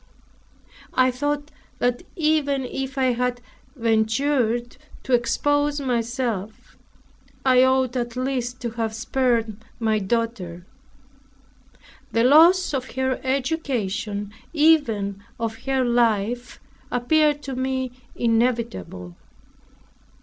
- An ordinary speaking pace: No, slow, 100 wpm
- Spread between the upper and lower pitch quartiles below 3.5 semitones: Yes, average, 2.8 semitones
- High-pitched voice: Yes, high, 245 Hz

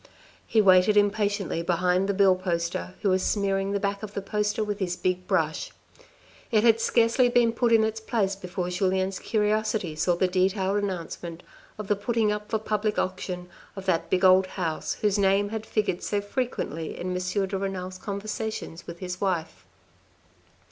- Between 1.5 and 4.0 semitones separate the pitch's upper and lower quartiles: Yes, narrow, 2.4 semitones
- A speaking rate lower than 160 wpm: No, average, 175 wpm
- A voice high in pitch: Yes, high, 195 Hz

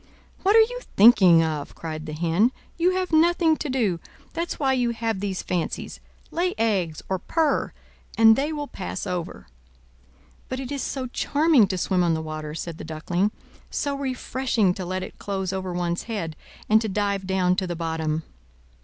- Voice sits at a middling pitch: No, high, 195 Hz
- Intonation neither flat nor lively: No, wide, 7.5 semitones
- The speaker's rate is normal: Yes, average, 180 wpm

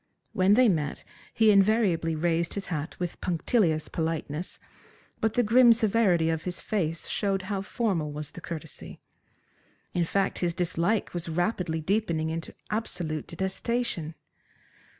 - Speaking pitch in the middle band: Yes, medium, 175 Hz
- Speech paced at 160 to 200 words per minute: No, slow, 135 wpm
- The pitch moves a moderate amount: Yes, average, 4.3 semitones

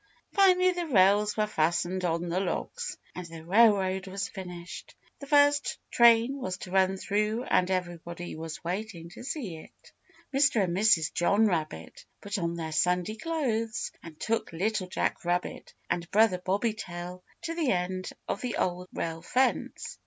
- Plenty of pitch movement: No, average, 4.4 semitones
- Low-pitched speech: No, high, 190 Hz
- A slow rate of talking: No, average, 160 wpm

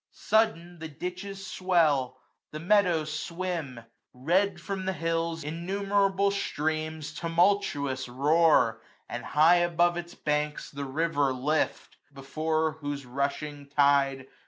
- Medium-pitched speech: Yes, medium, 160 Hz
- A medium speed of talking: No, slow, 115 wpm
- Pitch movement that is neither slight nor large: Yes, average, 3.6 semitones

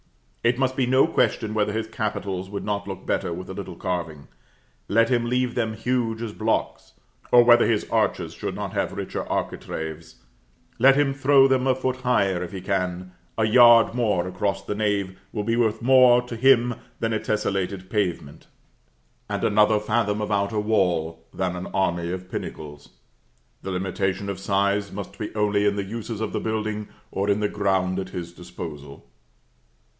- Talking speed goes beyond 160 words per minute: Yes, average, 180 wpm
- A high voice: No, low, 105 Hz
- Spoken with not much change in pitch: No, average, 3.7 semitones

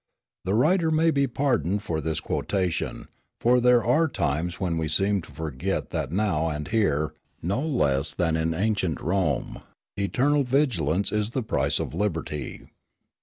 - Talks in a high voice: No, very low, 95 Hz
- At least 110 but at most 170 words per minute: Yes, average, 155 wpm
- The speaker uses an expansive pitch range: Yes, wide, 7.4 semitones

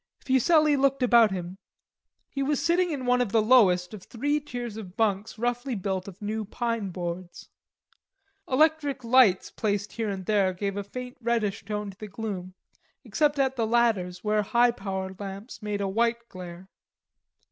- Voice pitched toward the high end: Yes, high, 220 Hz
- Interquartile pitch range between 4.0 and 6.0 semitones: Yes, average, 4.3 semitones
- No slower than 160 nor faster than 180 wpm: Yes, average, 170 wpm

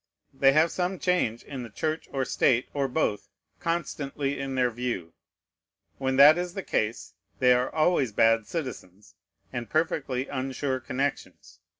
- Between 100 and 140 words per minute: No, average, 150 wpm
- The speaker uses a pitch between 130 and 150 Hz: Yes, low, 135 Hz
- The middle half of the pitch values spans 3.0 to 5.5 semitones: Yes, average, 3.9 semitones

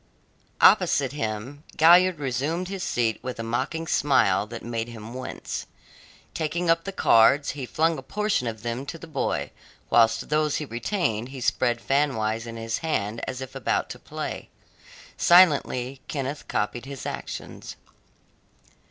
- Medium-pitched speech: No, low, 130 Hz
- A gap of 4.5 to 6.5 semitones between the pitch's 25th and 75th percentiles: Yes, average, 5.1 semitones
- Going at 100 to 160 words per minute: Yes, average, 150 wpm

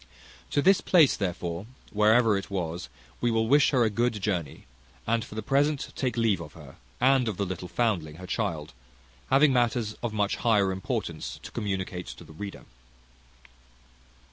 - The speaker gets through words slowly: No, average, 170 wpm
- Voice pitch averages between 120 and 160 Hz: No, low, 105 Hz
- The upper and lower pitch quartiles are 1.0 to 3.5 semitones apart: No, average, 4.8 semitones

